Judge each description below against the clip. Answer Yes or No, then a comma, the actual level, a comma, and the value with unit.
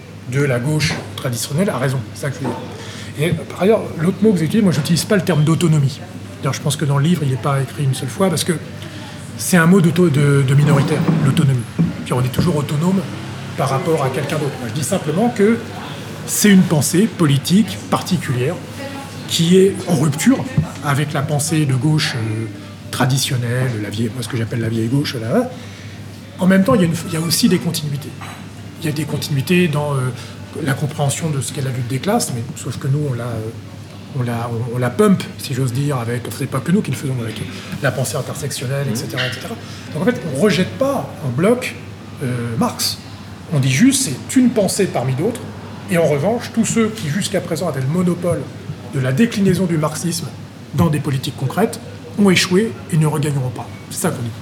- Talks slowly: No, average, 215 wpm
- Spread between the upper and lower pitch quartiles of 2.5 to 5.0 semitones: No, wide, 5.5 semitones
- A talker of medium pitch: Yes, medium, 145 Hz